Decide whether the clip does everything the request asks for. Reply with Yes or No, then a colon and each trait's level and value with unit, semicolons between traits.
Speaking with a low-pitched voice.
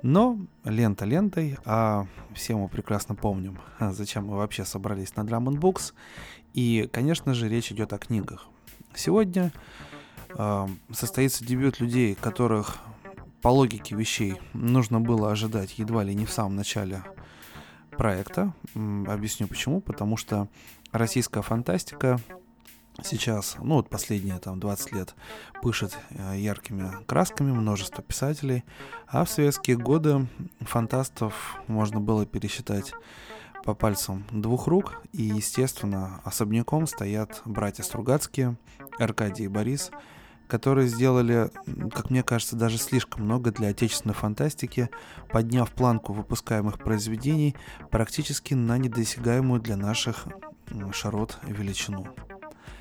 Yes: low, 115 Hz